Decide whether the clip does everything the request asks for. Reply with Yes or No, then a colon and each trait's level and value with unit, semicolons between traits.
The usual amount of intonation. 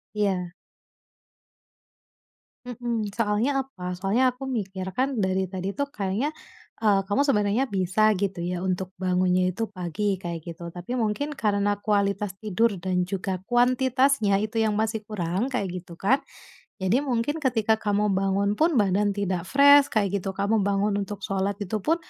Yes: average, 3.5 semitones